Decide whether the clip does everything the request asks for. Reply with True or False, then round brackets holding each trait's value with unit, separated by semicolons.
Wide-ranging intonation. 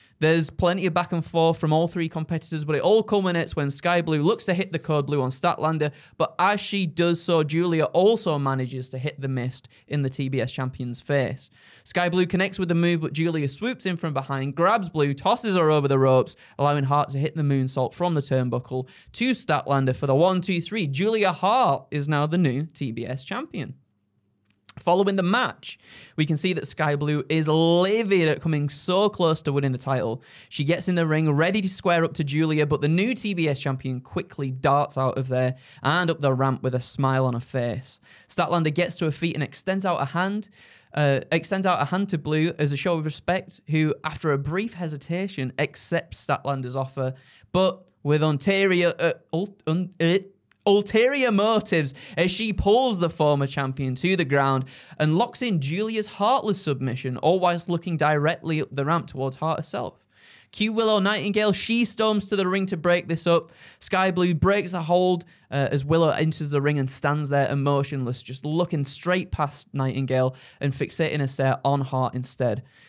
False (4.5 semitones)